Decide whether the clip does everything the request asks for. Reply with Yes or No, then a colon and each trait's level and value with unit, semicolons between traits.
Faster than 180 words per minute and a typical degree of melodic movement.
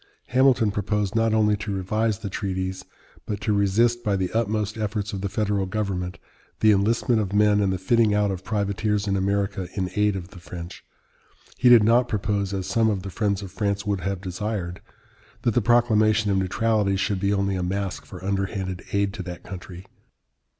No: average, 190 wpm; narrow, 2.2 semitones